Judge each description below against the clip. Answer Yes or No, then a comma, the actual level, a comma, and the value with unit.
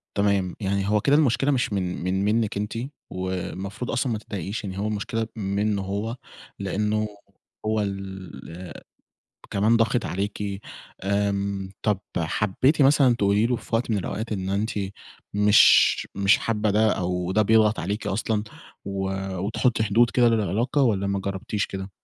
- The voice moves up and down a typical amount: No, narrow, 2.3 semitones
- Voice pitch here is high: No, low, 105 Hz